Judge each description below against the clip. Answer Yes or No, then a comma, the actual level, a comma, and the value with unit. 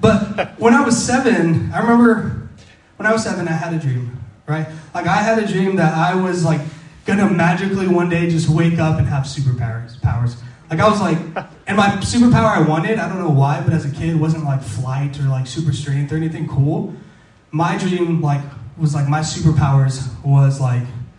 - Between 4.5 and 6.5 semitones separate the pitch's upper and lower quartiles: Yes, average, 5.0 semitones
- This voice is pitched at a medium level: Yes, medium, 155 Hz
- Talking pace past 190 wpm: Yes, fast, 205 wpm